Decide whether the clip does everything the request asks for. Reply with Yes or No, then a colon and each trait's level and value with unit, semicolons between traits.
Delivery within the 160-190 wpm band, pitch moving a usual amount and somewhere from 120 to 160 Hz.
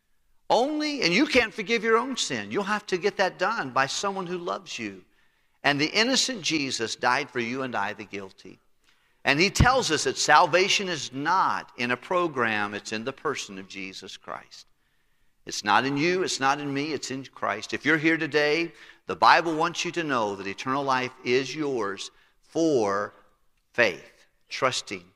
No: average, 185 wpm; wide, 8.9 semitones; medium, 140 Hz